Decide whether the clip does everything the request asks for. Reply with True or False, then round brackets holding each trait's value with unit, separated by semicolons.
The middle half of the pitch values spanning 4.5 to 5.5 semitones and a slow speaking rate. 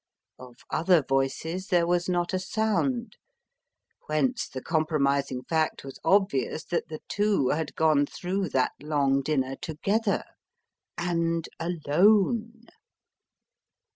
True (5.1 semitones; 110 wpm)